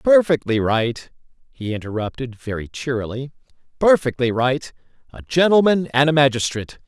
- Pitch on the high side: No, low, 135 Hz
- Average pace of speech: No, slow, 105 wpm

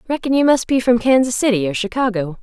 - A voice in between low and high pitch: No, high, 235 Hz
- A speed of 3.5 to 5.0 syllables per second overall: No, 6.3 syllables/s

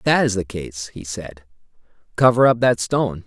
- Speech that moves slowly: No, average, 200 wpm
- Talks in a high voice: No, low, 105 Hz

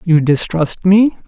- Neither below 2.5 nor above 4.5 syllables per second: Yes, 3.6 syllables/s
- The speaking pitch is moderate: Yes, medium, 175 Hz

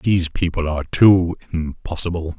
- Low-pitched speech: Yes, very low, 85 Hz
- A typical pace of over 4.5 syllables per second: Yes, 5.0 syllables/s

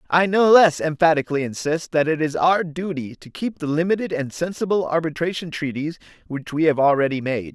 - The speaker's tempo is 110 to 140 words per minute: No, average, 185 wpm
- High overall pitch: No, medium, 160 Hz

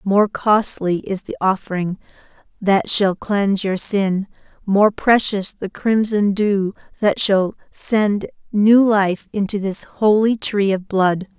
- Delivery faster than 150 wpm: No, slow, 135 wpm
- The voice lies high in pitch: Yes, high, 200 Hz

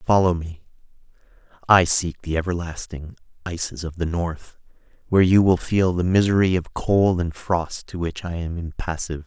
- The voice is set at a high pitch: No, very low, 85 Hz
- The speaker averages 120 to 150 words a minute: No, average, 160 wpm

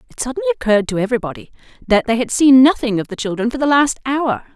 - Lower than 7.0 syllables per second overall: No, 7.2 syllables/s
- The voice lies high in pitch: Yes, high, 245 Hz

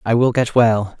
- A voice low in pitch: Yes, low, 115 Hz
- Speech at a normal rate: No, fast, 240 wpm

